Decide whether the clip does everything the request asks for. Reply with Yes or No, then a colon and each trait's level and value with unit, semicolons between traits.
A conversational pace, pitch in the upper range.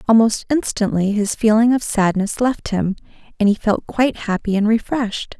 Yes: average, 165 wpm; high, 220 Hz